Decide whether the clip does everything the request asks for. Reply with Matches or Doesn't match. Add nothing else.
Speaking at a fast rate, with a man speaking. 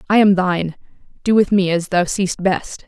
Doesn't match